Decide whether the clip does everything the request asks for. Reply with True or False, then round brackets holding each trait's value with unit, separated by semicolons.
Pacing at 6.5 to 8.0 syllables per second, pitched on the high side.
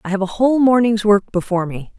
True (6.7 syllables/s; 210 Hz)